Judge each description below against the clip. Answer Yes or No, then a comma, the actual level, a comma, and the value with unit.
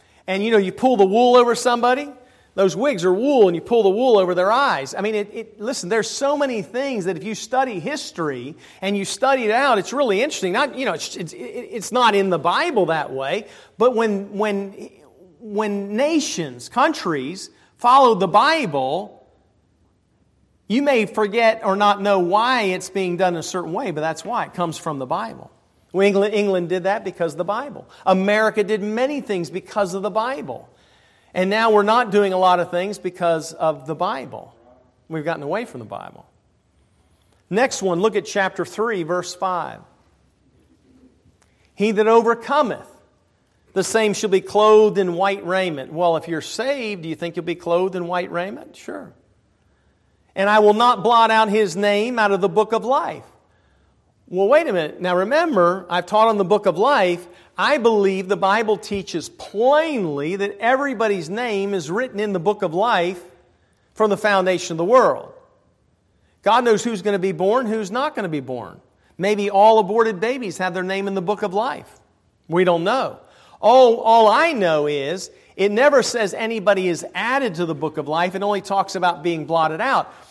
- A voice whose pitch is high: Yes, high, 200 Hz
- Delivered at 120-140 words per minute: No, average, 190 wpm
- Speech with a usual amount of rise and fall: Yes, average, 4.0 semitones